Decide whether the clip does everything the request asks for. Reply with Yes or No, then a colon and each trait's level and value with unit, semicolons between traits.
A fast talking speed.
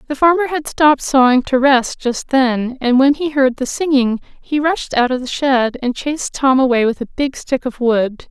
Yes: fast, 225 wpm